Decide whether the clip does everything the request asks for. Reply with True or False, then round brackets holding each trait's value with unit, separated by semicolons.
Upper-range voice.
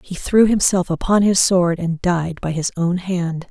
False (180 Hz)